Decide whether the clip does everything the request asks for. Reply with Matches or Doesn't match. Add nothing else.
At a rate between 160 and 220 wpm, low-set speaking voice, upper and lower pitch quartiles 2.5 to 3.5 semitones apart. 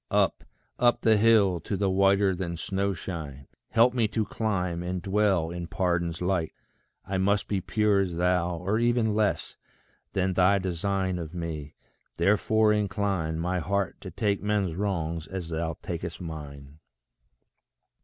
Doesn't match